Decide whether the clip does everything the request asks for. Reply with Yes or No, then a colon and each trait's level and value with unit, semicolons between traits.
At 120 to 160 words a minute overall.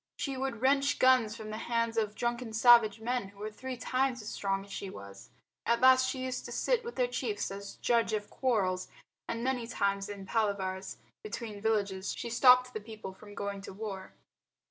No: average, 195 wpm